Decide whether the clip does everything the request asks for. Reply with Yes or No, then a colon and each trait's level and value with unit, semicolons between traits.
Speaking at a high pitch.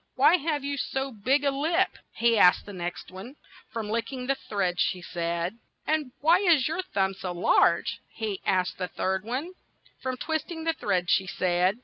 Yes: high, 235 Hz